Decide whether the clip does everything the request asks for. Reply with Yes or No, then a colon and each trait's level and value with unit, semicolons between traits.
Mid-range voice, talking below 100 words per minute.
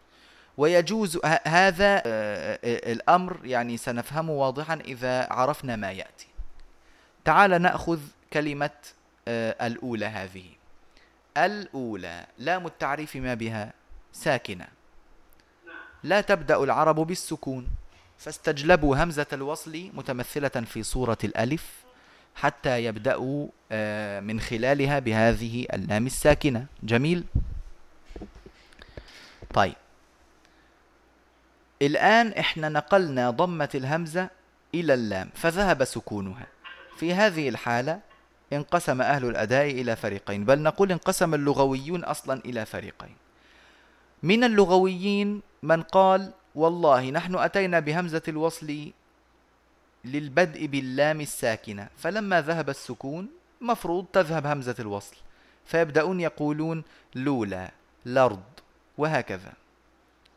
Yes: medium, 145 Hz; average, 90 wpm